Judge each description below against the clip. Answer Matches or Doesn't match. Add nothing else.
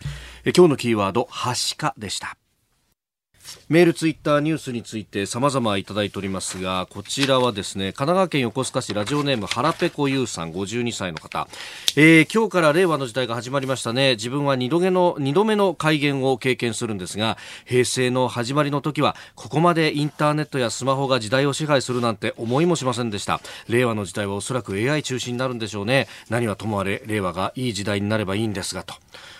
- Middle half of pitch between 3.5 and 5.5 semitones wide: Matches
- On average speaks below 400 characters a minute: Doesn't match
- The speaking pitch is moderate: Doesn't match